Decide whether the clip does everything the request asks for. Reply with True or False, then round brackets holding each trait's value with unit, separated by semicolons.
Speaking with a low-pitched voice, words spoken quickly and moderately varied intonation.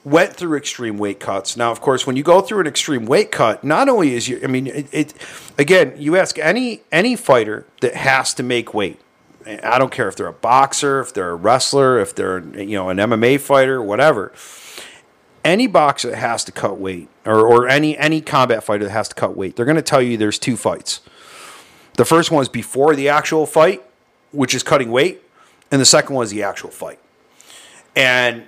True (130 Hz; 215 wpm; 4.0 semitones)